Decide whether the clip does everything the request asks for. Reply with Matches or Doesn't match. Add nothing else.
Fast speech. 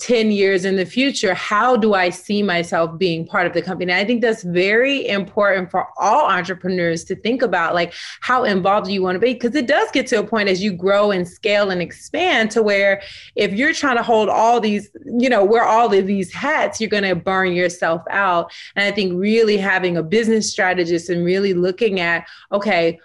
Matches